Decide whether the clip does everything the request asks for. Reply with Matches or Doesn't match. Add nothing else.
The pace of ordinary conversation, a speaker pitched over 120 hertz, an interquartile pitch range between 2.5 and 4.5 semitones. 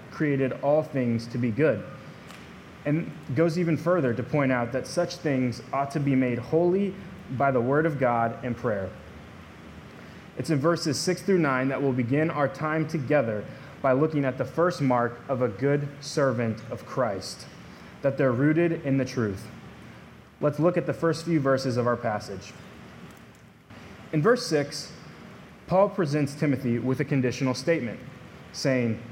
Matches